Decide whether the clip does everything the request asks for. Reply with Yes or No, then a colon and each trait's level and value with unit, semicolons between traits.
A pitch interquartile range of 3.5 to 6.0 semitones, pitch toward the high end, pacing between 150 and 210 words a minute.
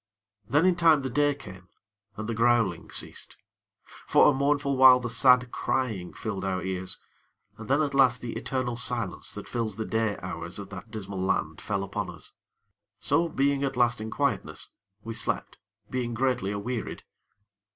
No: average, 4.1 semitones; low, 120 Hz; average, 170 wpm